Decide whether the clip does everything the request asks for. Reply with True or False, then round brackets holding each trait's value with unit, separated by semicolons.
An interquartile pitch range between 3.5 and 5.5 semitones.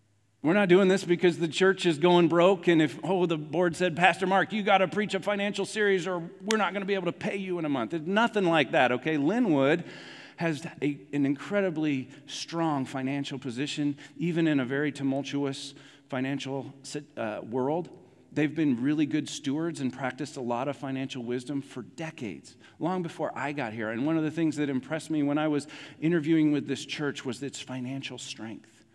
True (4.3 semitones)